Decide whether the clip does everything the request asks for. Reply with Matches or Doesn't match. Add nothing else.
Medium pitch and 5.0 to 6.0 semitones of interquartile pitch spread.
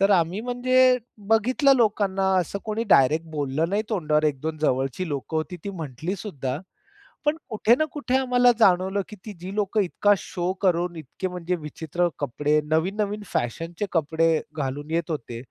Matches